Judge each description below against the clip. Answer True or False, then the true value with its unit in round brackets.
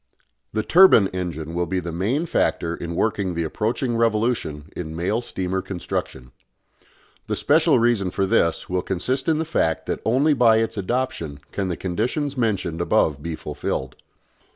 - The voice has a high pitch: False (95 Hz)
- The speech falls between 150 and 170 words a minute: True (160 wpm)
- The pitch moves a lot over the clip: True (5.8 semitones)